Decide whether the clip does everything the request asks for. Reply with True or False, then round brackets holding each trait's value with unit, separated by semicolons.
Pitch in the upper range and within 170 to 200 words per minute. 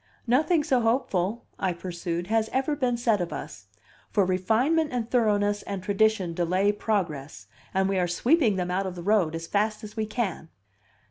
True (205 Hz; 180 wpm)